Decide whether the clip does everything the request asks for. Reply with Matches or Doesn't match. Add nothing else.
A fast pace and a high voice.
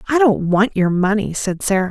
Matches